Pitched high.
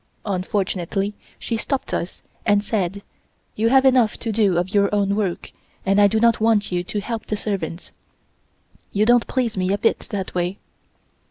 Yes: high, 205 Hz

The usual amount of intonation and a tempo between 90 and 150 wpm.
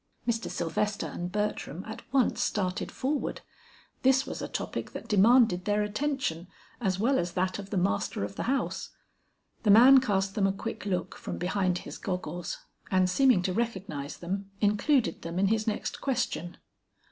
No: average, 4.2 semitones; average, 170 wpm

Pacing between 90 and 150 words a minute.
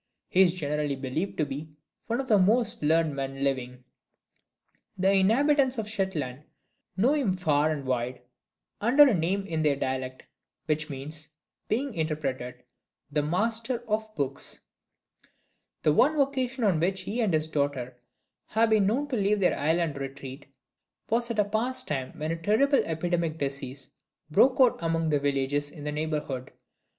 No: average, 160 wpm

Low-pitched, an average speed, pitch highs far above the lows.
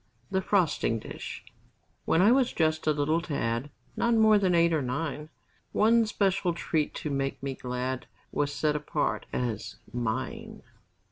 No: medium, 155 Hz; average, 150 wpm; wide, 5.9 semitones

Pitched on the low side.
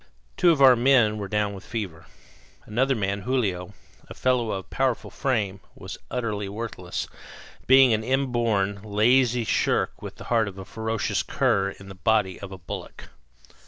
Yes: low, 110 Hz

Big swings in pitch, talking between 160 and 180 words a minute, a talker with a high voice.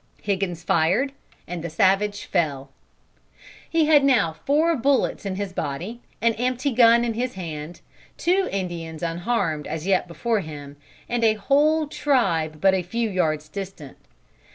No: wide, 6.6 semitones; average, 150 wpm; high, 195 Hz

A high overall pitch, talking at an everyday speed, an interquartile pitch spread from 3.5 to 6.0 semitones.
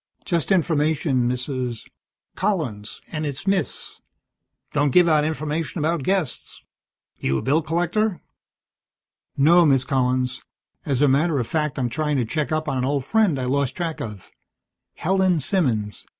No: medium, 150 Hz; average, 150 wpm; average, 4.5 semitones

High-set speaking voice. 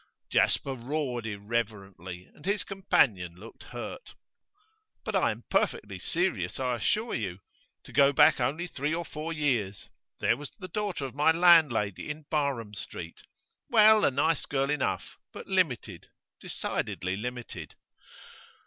No: low, 135 Hz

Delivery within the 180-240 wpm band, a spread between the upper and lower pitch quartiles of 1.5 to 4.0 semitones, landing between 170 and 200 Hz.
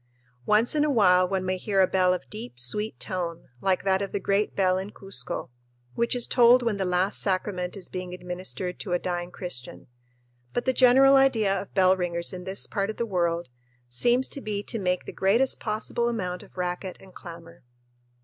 Yes: average, 200 wpm; average, 3.2 semitones; high, 190 Hz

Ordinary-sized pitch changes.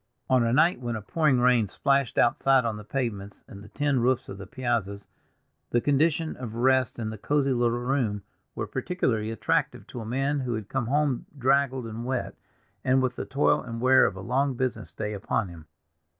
Yes: average, 3.4 semitones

